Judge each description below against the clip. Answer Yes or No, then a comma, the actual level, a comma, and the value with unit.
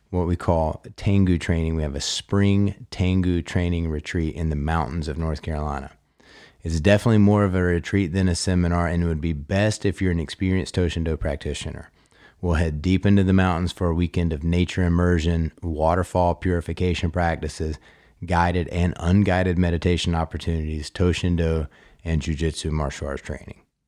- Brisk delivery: No, average, 160 wpm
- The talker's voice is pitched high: No, very low, 85 Hz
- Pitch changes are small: Yes, narrow, 2.3 semitones